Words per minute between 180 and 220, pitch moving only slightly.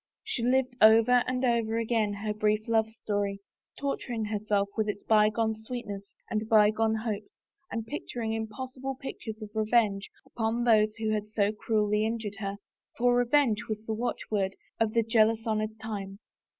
No: average, 155 wpm; narrow, 1.5 semitones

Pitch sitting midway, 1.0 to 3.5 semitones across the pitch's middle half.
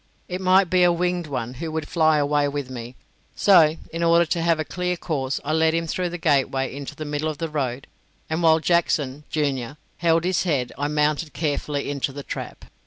Yes: medium, 155 Hz; average, 2.9 semitones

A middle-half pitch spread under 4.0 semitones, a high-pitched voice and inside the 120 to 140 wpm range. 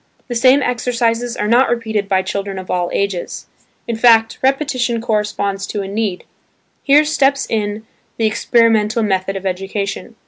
No: average, 3.3 semitones; high, 220 Hz; average, 150 wpm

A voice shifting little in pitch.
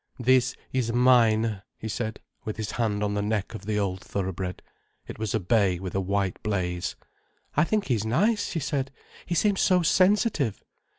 No: average, 4.5 semitones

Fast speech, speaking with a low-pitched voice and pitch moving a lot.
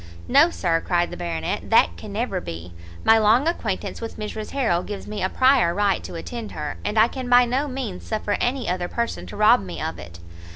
No: fast, 215 wpm; high, 210 Hz; wide, 6.1 semitones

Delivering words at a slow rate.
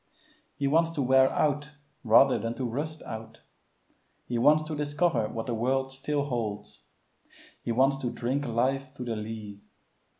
No: average, 160 wpm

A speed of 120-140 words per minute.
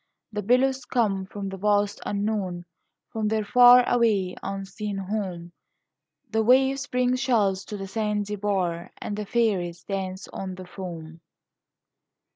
Yes: slow, 135 wpm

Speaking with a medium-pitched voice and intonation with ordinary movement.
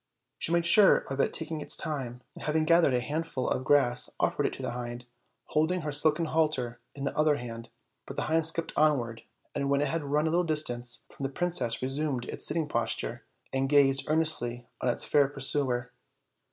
Yes: medium, 145 Hz; average, 4.1 semitones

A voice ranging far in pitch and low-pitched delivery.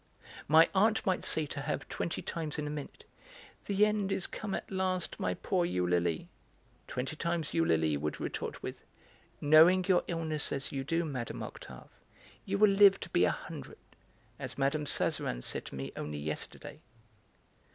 No: wide, 6.5 semitones; medium, 155 Hz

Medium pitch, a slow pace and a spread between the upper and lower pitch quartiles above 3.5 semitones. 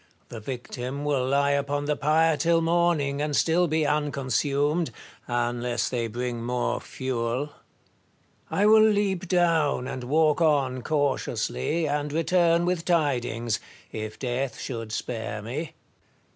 Yes: medium, 145 Hz; slow, 130 wpm; average, 4.7 semitones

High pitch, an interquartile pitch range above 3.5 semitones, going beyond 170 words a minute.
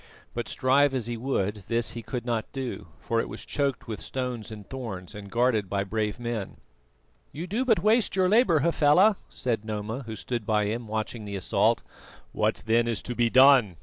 No: low, 120 Hz; average, 3.9 semitones; average, 195 wpm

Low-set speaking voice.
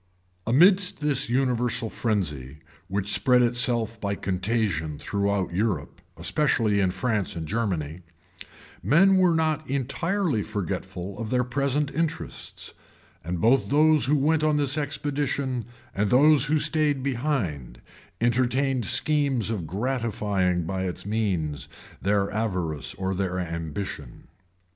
Yes: low, 115 Hz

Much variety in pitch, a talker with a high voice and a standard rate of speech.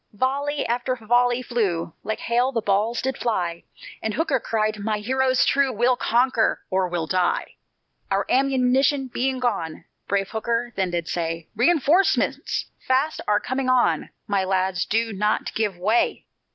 No: average, 4.7 semitones; high, 230 Hz; average, 150 wpm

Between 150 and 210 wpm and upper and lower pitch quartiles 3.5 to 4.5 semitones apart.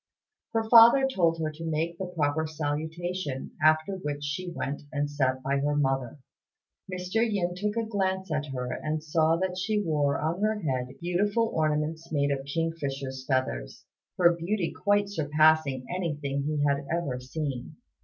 Yes: average, 160 wpm; average, 4.1 semitones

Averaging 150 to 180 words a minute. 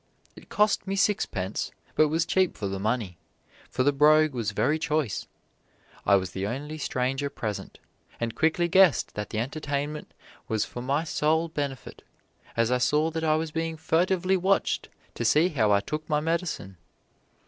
Yes: average, 170 wpm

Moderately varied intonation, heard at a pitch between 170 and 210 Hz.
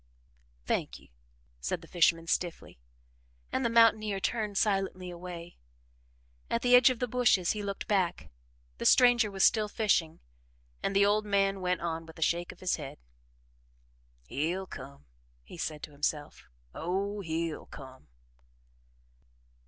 Yes: average, 4.3 semitones; medium, 185 Hz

